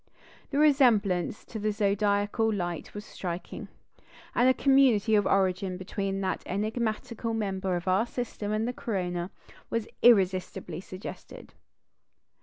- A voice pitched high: Yes, high, 205 Hz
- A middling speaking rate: No, slow, 125 wpm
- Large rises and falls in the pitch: No, average, 3.2 semitones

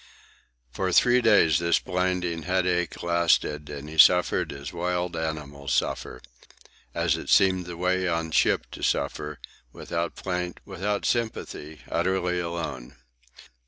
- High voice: No, very low, 85 Hz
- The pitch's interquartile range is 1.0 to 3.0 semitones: Yes, narrow, 2.6 semitones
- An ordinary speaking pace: No, slow, 125 wpm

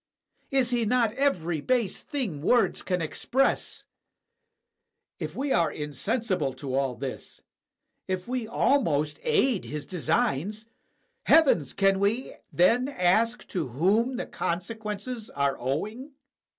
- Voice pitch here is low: No, high, 205 Hz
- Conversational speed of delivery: No, slow, 130 wpm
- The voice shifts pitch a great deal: Yes, wide, 7.6 semitones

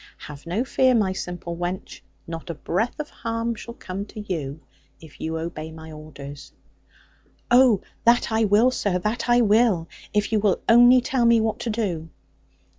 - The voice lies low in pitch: No, high, 205 Hz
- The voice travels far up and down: Yes, wide, 5.9 semitones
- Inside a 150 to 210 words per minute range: Yes, average, 175 wpm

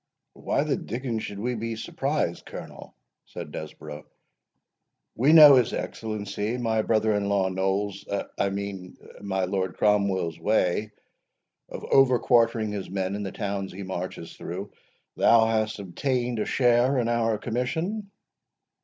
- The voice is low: Yes, low, 105 Hz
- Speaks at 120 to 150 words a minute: Yes, slow, 135 wpm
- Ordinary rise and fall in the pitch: Yes, average, 3.4 semitones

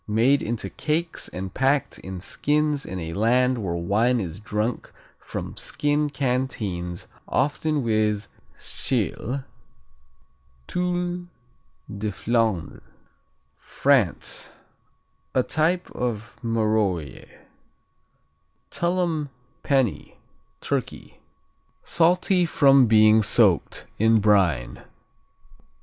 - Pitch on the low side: Yes, low, 120 Hz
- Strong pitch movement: Yes, wide, 5.9 semitones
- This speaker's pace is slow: Yes, slow, 85 wpm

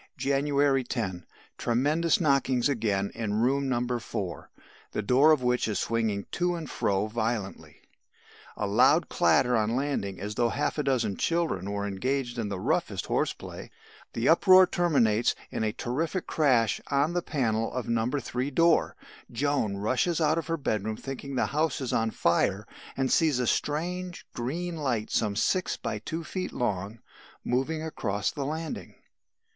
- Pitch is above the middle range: No, low, 125 Hz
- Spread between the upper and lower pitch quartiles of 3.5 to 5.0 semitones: No, wide, 5.5 semitones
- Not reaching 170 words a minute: Yes, average, 160 wpm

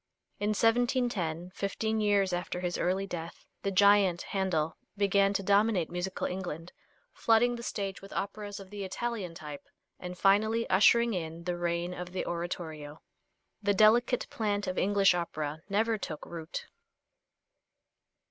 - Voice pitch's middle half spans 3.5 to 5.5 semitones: No, average, 3.0 semitones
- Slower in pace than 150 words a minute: Yes, average, 140 wpm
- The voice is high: Yes, high, 195 Hz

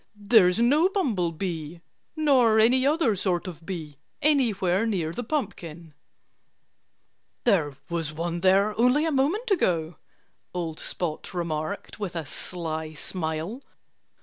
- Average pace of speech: No, slow, 120 wpm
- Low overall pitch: No, medium, 185 Hz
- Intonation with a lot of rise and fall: Yes, wide, 6.9 semitones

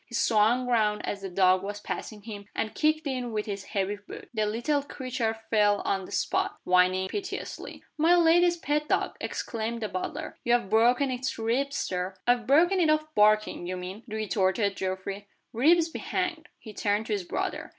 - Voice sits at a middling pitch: No, high, 220 Hz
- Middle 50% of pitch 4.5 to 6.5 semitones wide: Yes, wide, 5.6 semitones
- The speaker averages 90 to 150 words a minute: No, average, 180 wpm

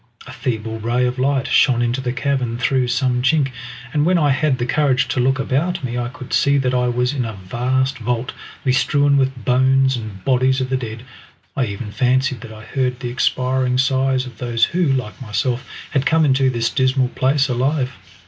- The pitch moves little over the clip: Yes, narrow, 1.7 semitones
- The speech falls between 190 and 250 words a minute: Yes, average, 200 wpm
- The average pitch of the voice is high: No, low, 130 Hz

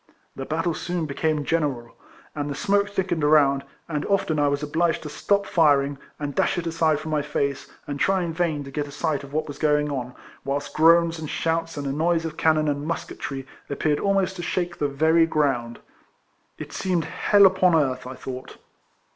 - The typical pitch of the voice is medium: Yes, medium, 155 Hz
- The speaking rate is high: No, average, 195 wpm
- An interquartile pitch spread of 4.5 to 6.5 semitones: No, average, 2.7 semitones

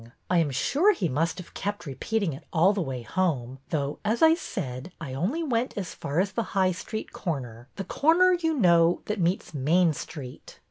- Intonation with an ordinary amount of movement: No, wide, 7.2 semitones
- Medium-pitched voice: Yes, medium, 175 Hz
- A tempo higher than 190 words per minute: Yes, average, 200 wpm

